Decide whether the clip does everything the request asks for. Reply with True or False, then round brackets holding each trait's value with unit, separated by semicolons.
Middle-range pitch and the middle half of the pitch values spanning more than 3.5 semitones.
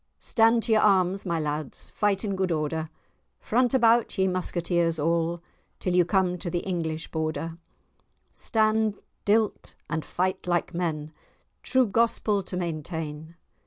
True (180 Hz; 4.2 semitones)